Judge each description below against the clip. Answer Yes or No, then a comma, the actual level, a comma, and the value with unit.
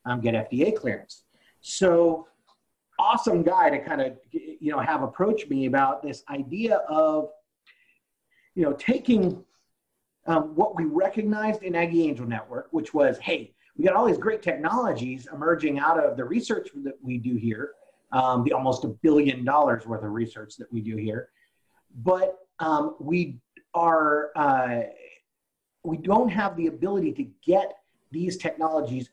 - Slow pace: No, average, 155 wpm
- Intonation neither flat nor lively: No, wide, 6.7 semitones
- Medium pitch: Yes, medium, 160 Hz